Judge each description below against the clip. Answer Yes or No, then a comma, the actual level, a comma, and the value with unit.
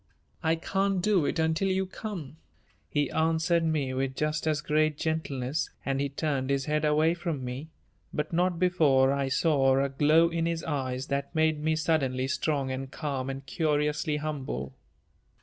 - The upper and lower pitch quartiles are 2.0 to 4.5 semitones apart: Yes, average, 3.0 semitones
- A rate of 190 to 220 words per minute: No, average, 165 wpm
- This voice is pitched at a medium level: Yes, medium, 150 Hz